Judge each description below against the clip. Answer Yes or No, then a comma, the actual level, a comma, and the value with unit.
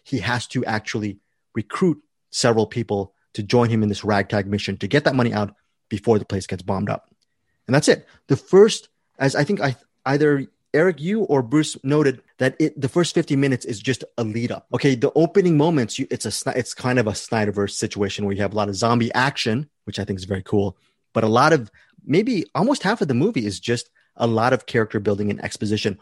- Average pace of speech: No, fast, 225 wpm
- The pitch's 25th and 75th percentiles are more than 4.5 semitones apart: Yes, average, 4.9 semitones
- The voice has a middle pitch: No, low, 120 Hz